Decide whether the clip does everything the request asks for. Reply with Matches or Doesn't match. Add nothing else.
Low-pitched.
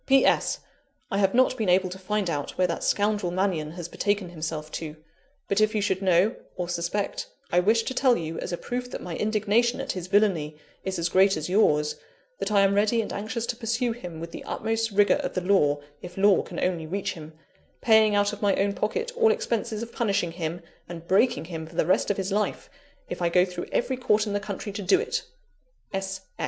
Doesn't match